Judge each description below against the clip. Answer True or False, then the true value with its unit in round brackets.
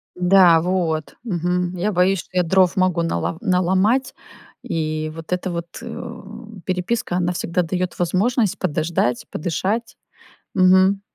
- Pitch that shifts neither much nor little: False (2.0 semitones)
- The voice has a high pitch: False (180 Hz)